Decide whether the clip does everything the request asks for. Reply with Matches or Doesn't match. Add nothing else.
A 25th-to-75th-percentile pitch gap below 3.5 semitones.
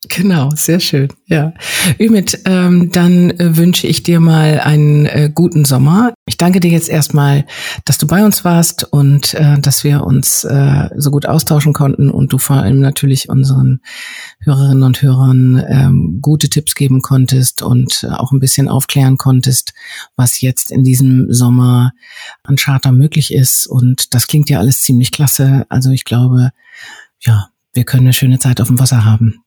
Matches